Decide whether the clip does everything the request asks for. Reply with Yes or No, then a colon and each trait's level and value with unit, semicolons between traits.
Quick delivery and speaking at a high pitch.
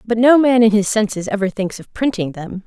Yes: fast, 250 wpm; high, 215 Hz